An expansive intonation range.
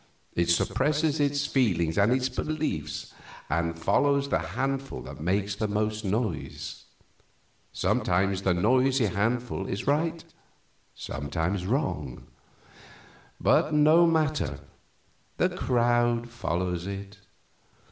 Yes: wide, 6.9 semitones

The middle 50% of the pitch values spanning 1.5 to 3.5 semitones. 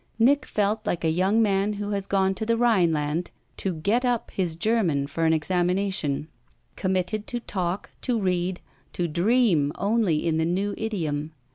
No: average, 4.5 semitones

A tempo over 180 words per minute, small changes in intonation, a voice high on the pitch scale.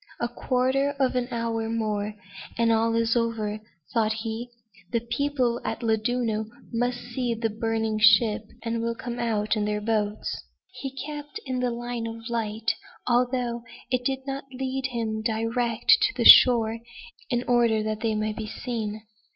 No: average, 160 wpm; narrow, 2.0 semitones; high, 230 Hz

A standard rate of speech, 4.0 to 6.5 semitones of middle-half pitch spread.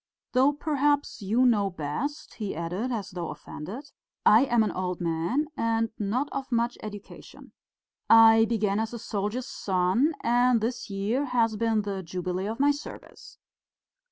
Yes: average, 155 wpm; average, 4.3 semitones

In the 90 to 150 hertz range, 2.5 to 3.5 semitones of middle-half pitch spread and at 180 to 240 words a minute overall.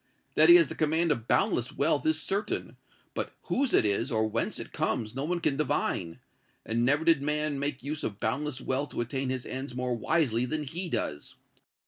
No: medium, 140 Hz; average, 4.5 semitones; average, 200 wpm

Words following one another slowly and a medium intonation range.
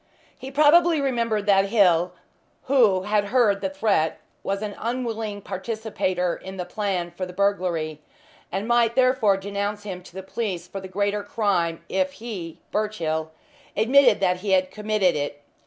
No: average, 155 wpm; average, 3.2 semitones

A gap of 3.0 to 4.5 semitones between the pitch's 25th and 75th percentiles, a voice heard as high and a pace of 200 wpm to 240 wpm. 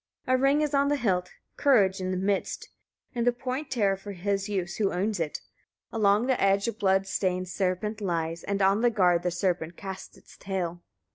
Yes: average, 3.5 semitones; high, 195 Hz; fast, 205 wpm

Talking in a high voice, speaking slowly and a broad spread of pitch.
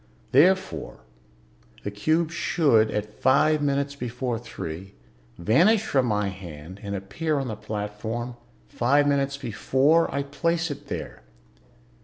No: low, 130 Hz; slow, 125 wpm; wide, 5.8 semitones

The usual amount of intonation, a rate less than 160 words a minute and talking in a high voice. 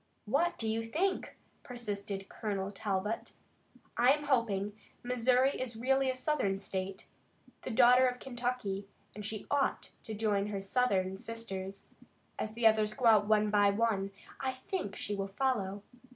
Yes: average, 3.9 semitones; average, 150 wpm; high, 220 Hz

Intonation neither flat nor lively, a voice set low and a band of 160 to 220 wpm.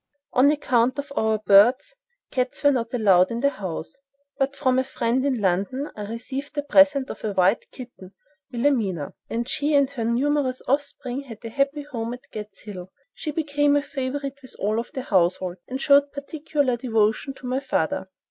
No: average, 4.6 semitones; very high, 255 Hz; average, 175 wpm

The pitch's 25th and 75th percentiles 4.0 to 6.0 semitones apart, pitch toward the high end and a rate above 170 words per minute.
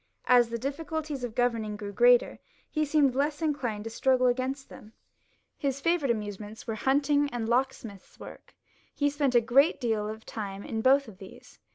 Yes: average, 4.3 semitones; very high, 250 Hz; average, 180 wpm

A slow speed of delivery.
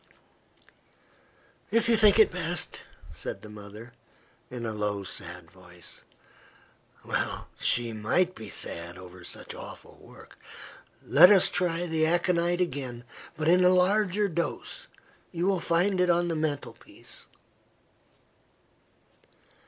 Yes: slow, 120 wpm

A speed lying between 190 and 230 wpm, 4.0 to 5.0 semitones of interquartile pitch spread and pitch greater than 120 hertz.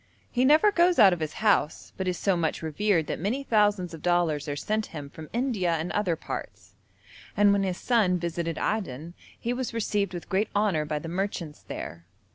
Yes: average, 200 wpm; average, 4.6 semitones; medium, 185 Hz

